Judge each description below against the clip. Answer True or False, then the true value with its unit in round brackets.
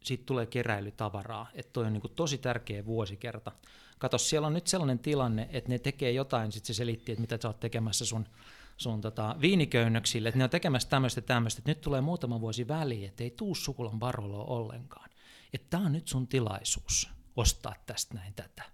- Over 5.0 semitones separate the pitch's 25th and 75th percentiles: False (2.9 semitones)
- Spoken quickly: True (190 wpm)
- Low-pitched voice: True (120 Hz)